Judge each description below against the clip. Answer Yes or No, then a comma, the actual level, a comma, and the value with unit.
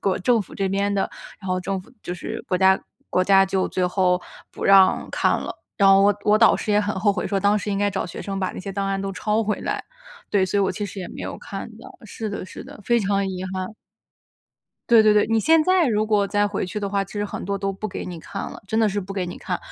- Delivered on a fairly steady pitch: Yes, narrow, 1.6 semitones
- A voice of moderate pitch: No, high, 200 Hz